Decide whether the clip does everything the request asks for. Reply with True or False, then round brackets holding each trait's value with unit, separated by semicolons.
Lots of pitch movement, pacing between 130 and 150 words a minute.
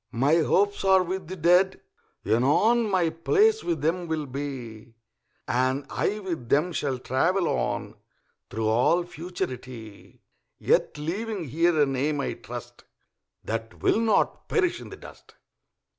True (6.3 semitones; 140 wpm)